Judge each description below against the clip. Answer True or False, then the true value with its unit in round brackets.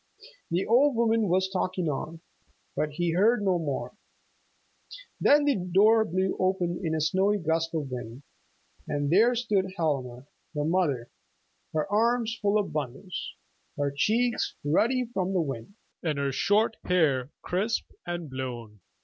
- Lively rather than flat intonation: True (6.1 semitones)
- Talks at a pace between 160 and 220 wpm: False (145 wpm)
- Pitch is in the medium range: True (180 Hz)